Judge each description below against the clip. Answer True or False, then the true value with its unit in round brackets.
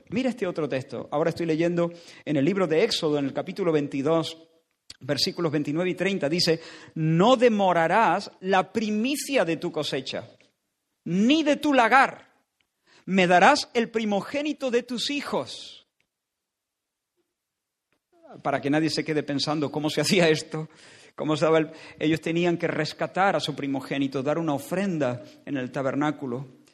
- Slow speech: False (145 wpm)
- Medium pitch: True (165 Hz)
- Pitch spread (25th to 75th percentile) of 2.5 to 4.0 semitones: False (4.5 semitones)